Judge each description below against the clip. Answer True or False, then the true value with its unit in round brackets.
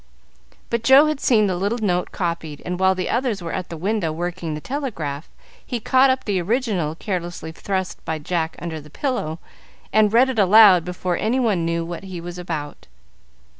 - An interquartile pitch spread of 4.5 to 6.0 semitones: True (4.9 semitones)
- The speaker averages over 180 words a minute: True (190 wpm)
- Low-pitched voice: False (185 Hz)